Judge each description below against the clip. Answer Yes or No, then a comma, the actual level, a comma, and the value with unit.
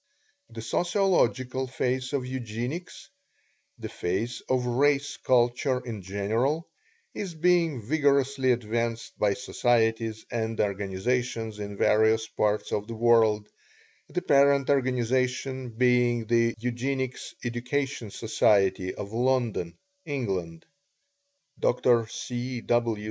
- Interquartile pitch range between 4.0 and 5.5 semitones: No, average, 2.9 semitones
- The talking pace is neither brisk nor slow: No, slow, 105 wpm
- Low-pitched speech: Yes, low, 120 Hz